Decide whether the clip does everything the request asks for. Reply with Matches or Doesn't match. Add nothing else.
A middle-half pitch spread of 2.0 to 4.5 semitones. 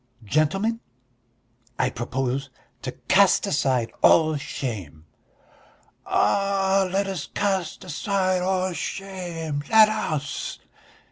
Doesn't match